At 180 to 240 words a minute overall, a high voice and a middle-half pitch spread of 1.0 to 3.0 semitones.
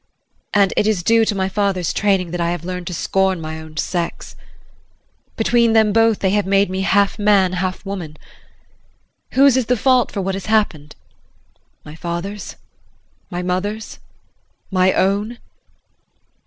No: average, 155 wpm; high, 195 Hz; average, 2.7 semitones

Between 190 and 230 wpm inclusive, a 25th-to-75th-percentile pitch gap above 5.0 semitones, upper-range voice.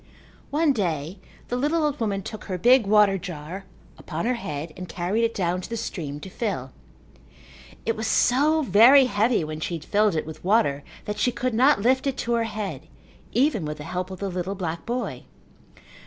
Yes: average, 200 wpm; wide, 5.6 semitones; high, 205 Hz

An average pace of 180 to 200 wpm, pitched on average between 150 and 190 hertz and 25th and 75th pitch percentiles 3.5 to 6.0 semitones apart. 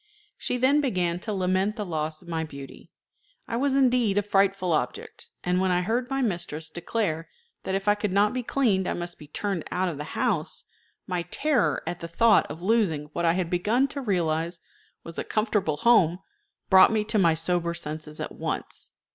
Yes: average, 195 wpm; medium, 185 Hz; average, 4.5 semitones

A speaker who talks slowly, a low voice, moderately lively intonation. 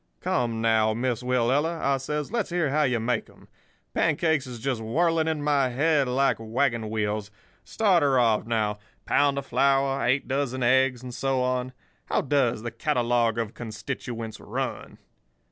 No: average, 160 wpm; low, 130 Hz; average, 3.5 semitones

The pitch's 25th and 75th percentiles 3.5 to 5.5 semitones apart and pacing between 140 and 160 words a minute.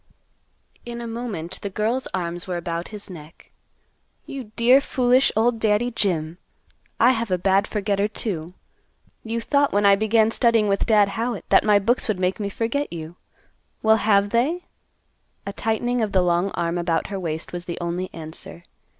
No: average, 4.6 semitones; average, 175 wpm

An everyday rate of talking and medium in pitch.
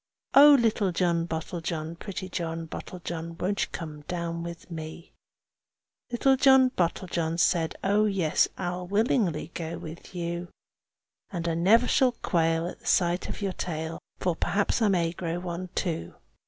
Yes: average, 155 wpm; medium, 175 Hz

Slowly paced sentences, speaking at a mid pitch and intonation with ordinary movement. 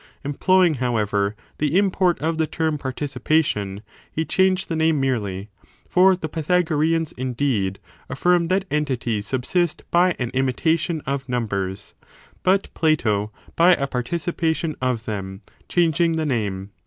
No: slow, 130 wpm; medium, 145 Hz; wide, 6.0 semitones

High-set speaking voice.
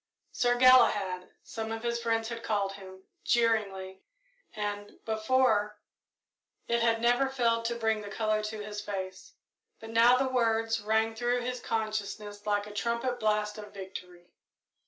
Yes: high, 220 Hz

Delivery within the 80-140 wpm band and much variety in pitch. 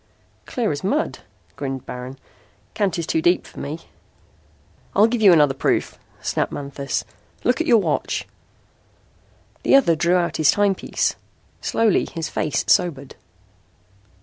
Yes: slow, 135 wpm; wide, 7.3 semitones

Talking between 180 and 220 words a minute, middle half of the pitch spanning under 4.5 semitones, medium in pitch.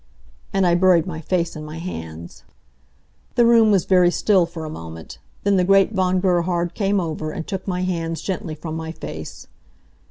Yes: average, 185 wpm; average, 2.9 semitones; medium, 175 Hz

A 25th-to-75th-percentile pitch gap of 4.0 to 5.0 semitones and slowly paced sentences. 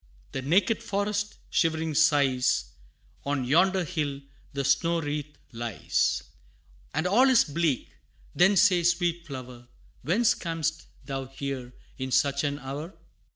Yes: average, 4.3 semitones; slow, 125 wpm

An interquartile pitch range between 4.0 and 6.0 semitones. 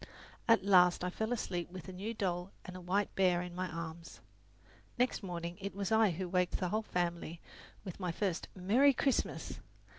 No: narrow, 2.4 semitones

